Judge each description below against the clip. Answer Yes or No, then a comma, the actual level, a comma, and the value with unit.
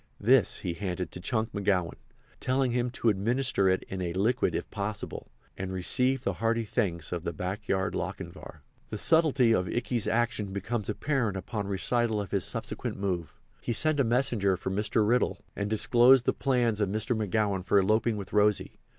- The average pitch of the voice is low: Yes, low, 105 Hz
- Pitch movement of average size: Yes, average, 3.8 semitones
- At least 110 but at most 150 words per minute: No, average, 175 wpm